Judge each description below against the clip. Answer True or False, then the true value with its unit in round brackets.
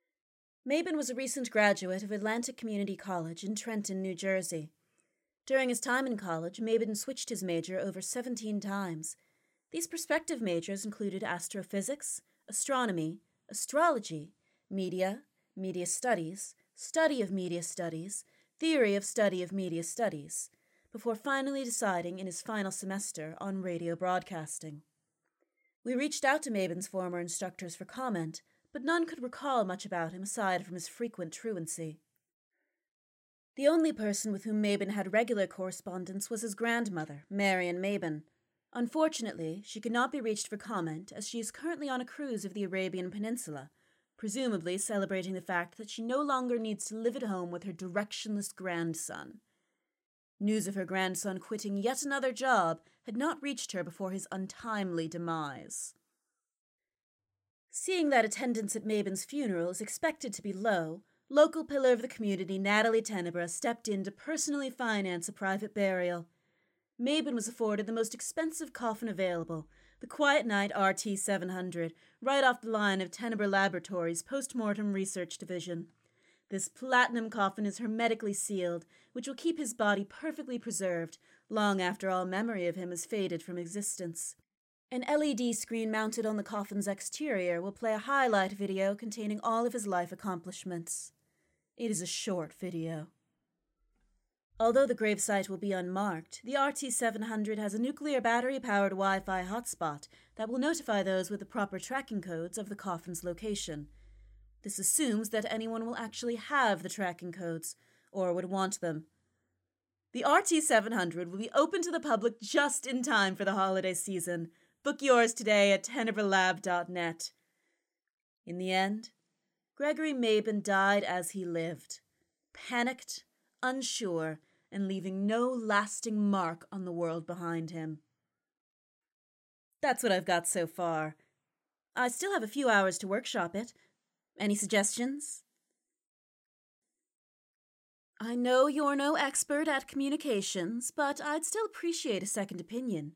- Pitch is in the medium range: False (200 Hz)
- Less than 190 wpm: True (150 wpm)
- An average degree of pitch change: True (4.8 semitones)